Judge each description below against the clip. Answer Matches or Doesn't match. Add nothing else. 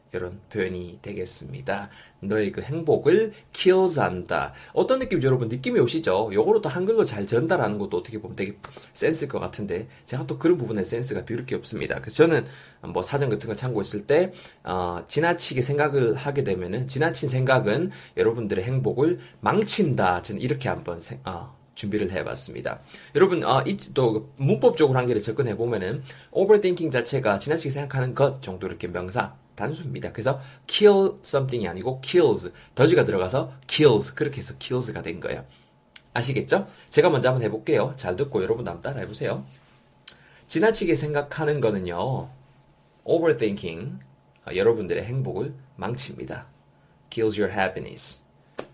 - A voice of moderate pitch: Doesn't match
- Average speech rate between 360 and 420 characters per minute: Matches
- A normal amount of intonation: Doesn't match